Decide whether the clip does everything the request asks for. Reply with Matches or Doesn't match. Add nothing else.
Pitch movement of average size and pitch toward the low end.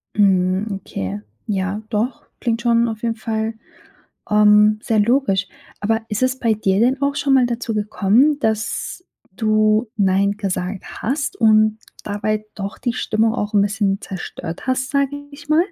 Doesn't match